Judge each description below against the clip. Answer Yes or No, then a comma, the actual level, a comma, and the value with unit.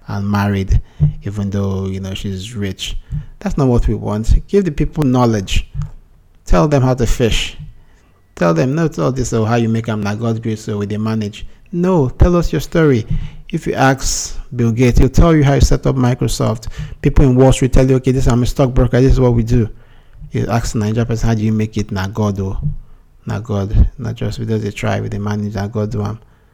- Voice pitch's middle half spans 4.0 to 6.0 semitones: Yes, average, 4.3 semitones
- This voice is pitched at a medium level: No, low, 115 Hz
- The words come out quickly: Yes, fast, 215 wpm